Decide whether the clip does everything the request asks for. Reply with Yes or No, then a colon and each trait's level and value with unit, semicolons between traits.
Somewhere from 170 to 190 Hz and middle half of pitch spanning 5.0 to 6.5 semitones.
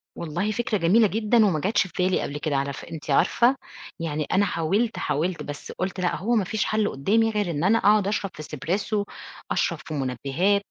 Yes: medium, 185 Hz; wide, 5.4 semitones